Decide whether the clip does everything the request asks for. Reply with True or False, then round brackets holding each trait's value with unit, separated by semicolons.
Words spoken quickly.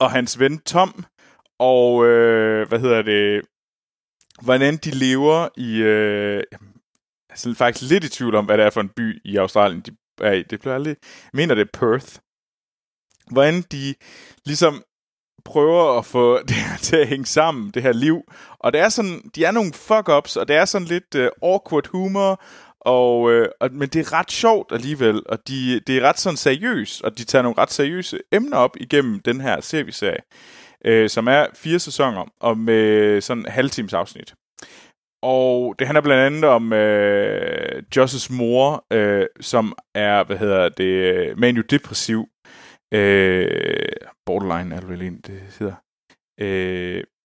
False (165 wpm)